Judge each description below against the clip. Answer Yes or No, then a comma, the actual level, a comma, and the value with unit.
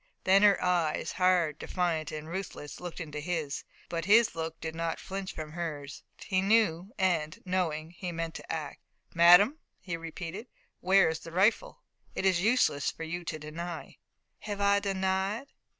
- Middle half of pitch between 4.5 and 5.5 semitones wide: No, average, 3.0 semitones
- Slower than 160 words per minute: No, average, 165 wpm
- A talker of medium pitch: Yes, medium, 175 Hz